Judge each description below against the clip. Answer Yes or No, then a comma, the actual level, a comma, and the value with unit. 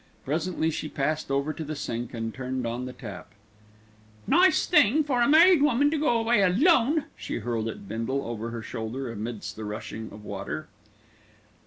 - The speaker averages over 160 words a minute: Yes, average, 175 wpm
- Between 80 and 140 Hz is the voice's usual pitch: Yes, low, 135 Hz